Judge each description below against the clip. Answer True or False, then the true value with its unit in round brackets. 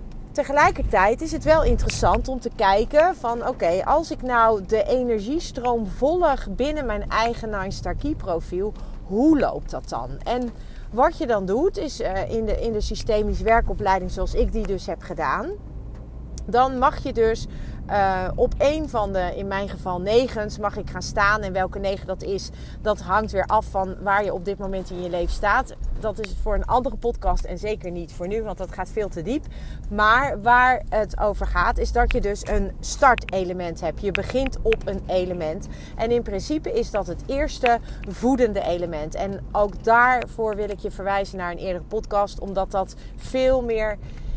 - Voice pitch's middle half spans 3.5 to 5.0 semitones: True (4.1 semitones)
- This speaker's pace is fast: False (190 wpm)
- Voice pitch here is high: True (210 Hz)